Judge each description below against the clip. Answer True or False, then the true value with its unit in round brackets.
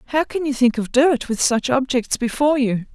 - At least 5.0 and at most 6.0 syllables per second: True (5.3 syllables/s)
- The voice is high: True (260 Hz)